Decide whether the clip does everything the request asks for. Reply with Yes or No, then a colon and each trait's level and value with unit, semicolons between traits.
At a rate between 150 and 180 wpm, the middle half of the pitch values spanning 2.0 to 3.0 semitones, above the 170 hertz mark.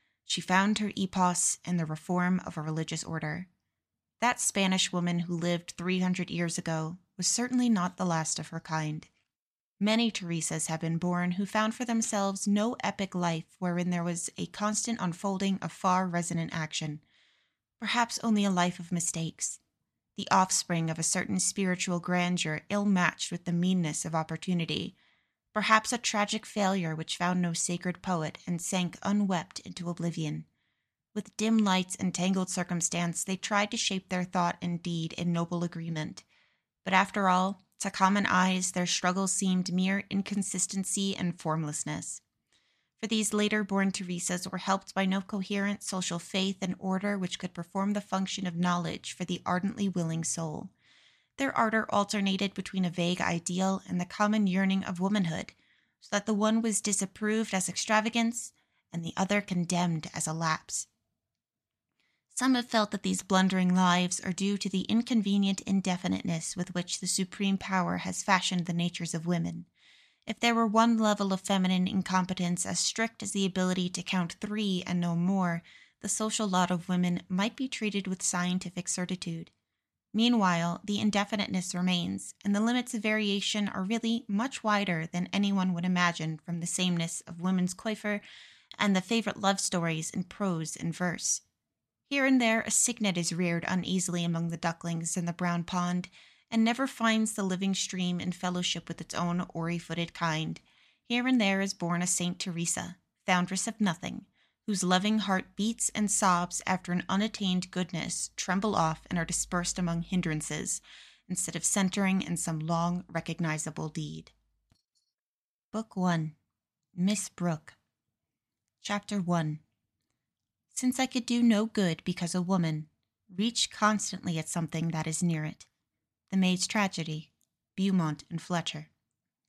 Yes: average, 160 wpm; average, 2.7 semitones; medium, 185 Hz